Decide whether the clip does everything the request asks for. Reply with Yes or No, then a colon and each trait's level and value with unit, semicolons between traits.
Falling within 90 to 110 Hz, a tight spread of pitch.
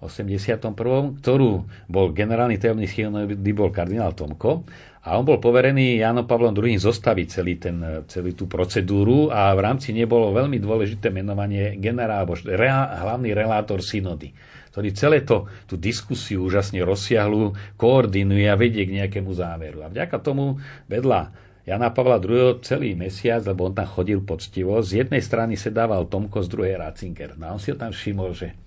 No: low, 105 Hz; average, 3.6 semitones